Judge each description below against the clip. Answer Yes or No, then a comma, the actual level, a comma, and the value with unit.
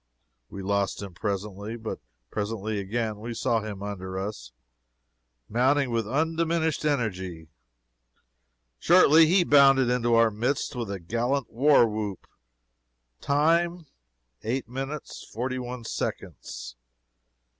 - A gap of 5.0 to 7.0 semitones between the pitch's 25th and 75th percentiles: Yes, wide, 5.4 semitones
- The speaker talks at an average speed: No, slow, 115 wpm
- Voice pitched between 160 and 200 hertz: No, low, 115 Hz